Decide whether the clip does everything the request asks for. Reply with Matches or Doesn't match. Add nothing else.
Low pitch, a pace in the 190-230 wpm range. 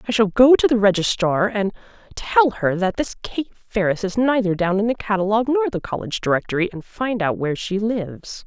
Doesn't match